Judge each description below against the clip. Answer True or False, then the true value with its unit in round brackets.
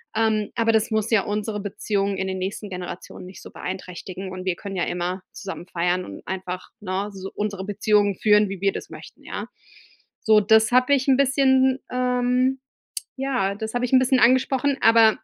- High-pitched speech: True (210 Hz)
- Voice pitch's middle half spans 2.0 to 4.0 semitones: False (4.6 semitones)